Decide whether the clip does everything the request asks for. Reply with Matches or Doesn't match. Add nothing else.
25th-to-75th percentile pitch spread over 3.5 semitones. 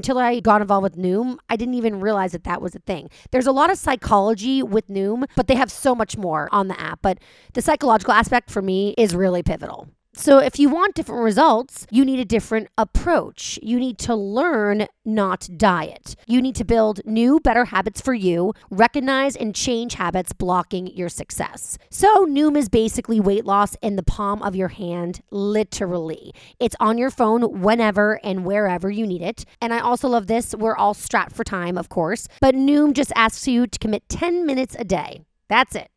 Matches